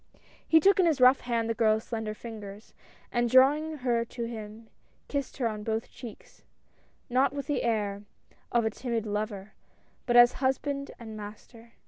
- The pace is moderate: Yes, average, 170 wpm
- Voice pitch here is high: Yes, high, 235 Hz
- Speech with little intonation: No, average, 3.1 semitones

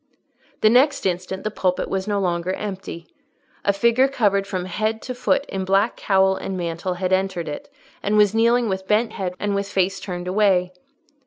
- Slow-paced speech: No, average, 185 wpm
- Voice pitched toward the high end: Yes, high, 195 Hz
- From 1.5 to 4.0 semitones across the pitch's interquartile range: Yes, narrow, 2.6 semitones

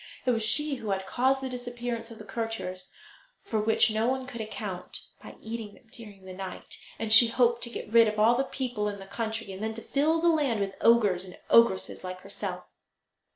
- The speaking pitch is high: Yes, high, 225 Hz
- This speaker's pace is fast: Yes, fast, 215 wpm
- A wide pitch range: No, average, 2.8 semitones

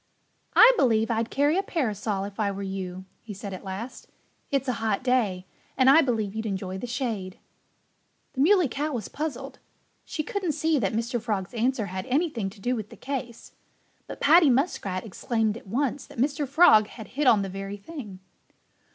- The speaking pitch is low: No, high, 230 Hz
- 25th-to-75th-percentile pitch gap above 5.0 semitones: Yes, wide, 5.6 semitones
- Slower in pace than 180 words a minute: No, average, 185 wpm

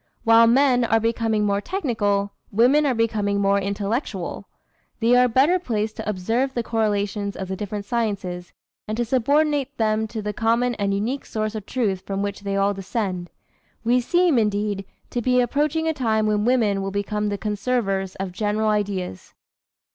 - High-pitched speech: Yes, high, 215 Hz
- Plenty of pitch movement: No, average, 3.3 semitones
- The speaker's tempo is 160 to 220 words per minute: Yes, average, 170 wpm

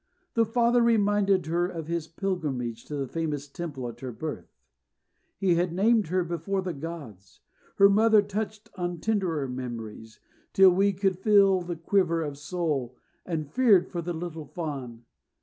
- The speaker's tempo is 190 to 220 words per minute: No, average, 160 wpm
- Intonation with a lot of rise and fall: No, average, 4.9 semitones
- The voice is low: No, medium, 175 Hz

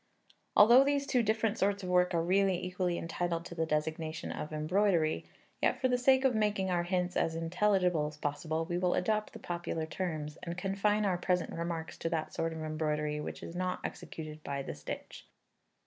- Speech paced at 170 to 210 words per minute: Yes, average, 195 wpm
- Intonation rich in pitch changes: No, average, 3.6 semitones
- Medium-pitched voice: Yes, medium, 175 Hz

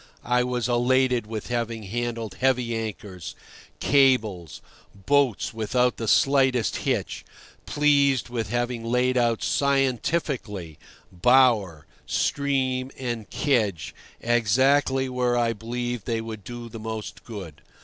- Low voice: Yes, low, 120 Hz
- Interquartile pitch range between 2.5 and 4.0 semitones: Yes, average, 2.9 semitones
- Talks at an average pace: No, slow, 110 wpm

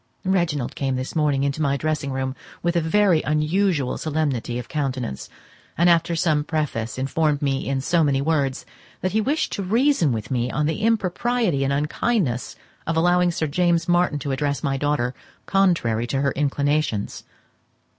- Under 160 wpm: No, average, 165 wpm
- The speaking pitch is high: No, medium, 150 Hz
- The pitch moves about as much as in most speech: Yes, average, 4.1 semitones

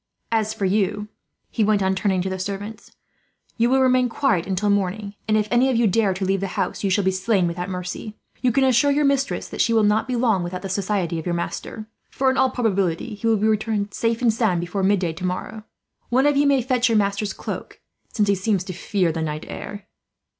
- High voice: Yes, high, 210 Hz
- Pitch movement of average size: Yes, average, 3.5 semitones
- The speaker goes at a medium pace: No, fast, 230 wpm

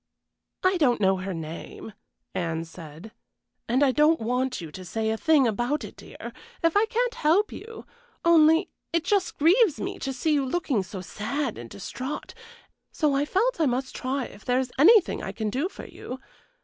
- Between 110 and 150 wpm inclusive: No, average, 190 wpm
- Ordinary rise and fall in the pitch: No, wide, 7.3 semitones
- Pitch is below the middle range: No, very high, 270 Hz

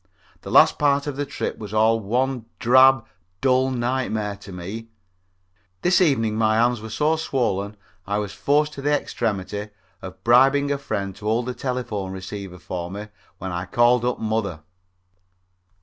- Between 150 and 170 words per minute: Yes, average, 165 wpm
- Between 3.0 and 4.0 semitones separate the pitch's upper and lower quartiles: No, average, 4.5 semitones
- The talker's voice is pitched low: Yes, low, 115 Hz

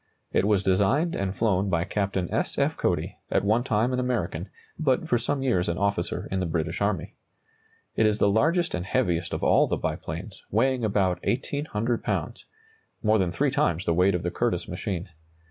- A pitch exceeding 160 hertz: No, low, 100 Hz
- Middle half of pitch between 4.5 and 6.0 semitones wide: Yes, average, 4.9 semitones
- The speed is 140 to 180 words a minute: No, average, 190 wpm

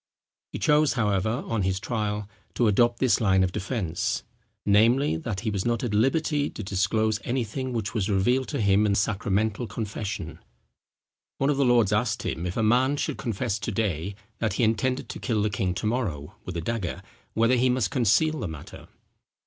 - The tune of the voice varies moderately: Yes, average, 3.7 semitones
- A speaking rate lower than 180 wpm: No, average, 190 wpm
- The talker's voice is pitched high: No, low, 110 Hz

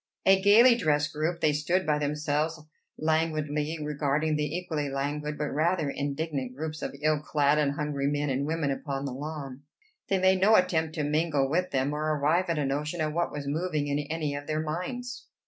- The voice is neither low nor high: Yes, medium, 150 Hz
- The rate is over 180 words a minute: Yes, average, 195 wpm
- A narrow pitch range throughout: Yes, narrow, 2.0 semitones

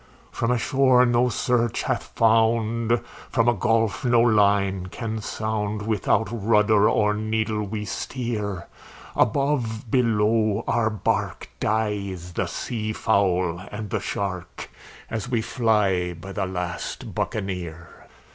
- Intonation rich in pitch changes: No, narrow, 2.6 semitones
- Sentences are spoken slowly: Yes, slow, 125 wpm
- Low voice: Yes, low, 110 Hz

